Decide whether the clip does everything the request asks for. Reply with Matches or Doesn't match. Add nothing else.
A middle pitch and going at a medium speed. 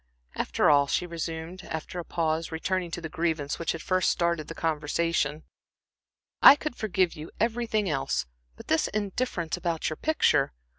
Matches